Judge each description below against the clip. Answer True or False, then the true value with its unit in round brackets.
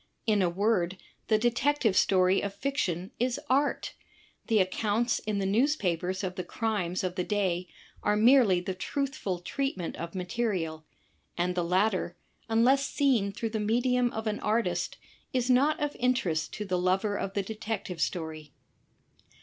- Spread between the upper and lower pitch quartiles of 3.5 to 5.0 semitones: True (4.6 semitones)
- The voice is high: True (205 Hz)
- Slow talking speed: False (160 wpm)